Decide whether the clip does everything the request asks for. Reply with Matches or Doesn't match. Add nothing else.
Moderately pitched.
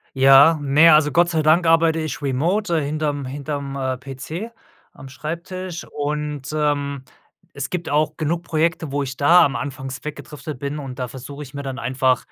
Matches